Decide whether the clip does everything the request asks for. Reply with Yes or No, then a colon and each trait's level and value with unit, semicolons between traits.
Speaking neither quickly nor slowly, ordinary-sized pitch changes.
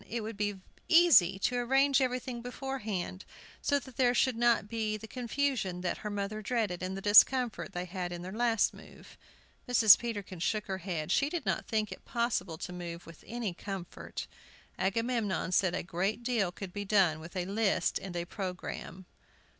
Yes: average, 180 wpm; average, 4.6 semitones